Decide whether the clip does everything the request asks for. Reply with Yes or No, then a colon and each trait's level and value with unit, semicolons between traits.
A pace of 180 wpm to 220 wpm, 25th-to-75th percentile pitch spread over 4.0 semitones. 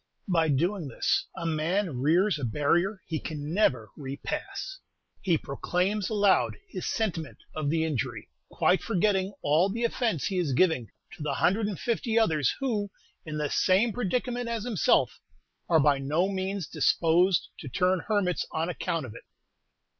No: average, 160 wpm; average, 5.1 semitones